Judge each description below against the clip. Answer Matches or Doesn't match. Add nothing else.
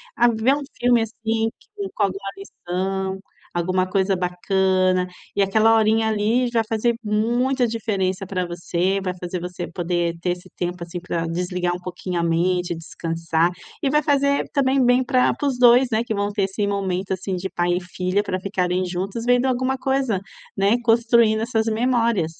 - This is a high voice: Matches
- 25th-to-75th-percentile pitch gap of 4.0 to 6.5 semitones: Matches